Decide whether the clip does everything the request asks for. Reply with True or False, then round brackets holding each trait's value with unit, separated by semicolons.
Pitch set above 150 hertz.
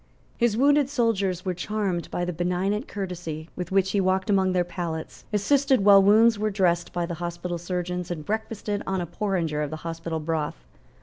True (185 Hz)